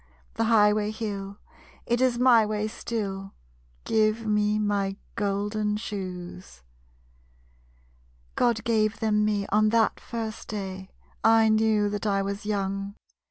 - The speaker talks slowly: Yes, slow, 120 wpm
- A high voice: Yes, high, 210 Hz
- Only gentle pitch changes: Yes, narrow, 1.7 semitones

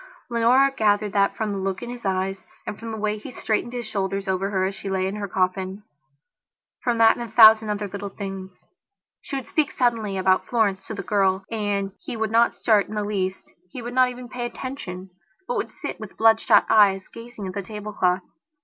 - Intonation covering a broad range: No, average, 3.0 semitones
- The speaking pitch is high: Yes, high, 210 Hz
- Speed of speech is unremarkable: No, fast, 210 wpm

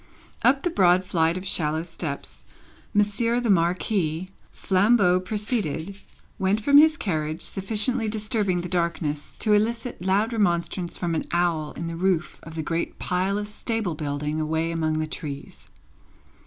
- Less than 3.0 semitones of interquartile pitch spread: No, average, 4.3 semitones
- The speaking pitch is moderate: Yes, medium, 180 Hz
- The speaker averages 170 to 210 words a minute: No, average, 150 wpm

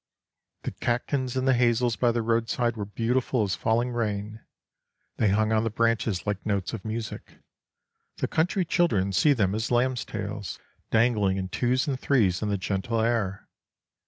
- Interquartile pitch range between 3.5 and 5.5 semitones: No, average, 3.0 semitones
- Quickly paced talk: No, average, 165 wpm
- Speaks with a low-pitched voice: Yes, low, 115 Hz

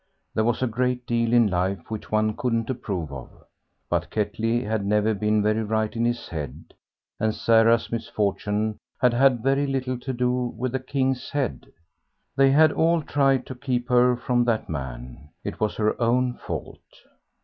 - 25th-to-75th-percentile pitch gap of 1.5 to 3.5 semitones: Yes, average, 2.9 semitones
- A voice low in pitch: Yes, low, 115 Hz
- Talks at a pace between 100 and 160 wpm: No, average, 170 wpm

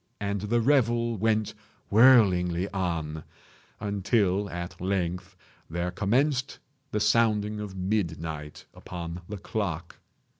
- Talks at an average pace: No, slow, 105 wpm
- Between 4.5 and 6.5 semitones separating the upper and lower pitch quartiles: No, average, 3.6 semitones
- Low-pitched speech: Yes, low, 100 Hz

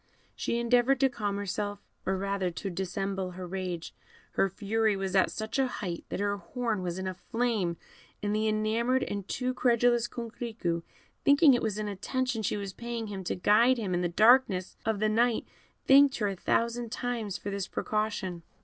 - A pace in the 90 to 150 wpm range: No, average, 185 wpm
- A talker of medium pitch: No, high, 215 Hz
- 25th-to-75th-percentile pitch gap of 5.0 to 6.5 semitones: No, average, 3.7 semitones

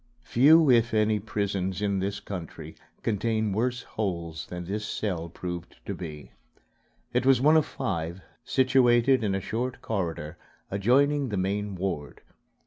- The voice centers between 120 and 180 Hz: No, low, 105 Hz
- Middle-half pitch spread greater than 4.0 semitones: Yes, average, 4.9 semitones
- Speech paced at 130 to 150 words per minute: Yes, average, 140 wpm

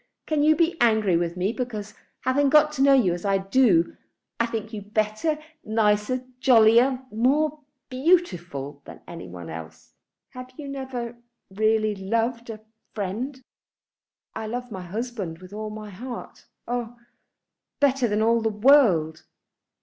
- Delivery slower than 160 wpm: Yes, average, 145 wpm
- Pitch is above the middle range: Yes, high, 225 Hz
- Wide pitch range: No, average, 4.3 semitones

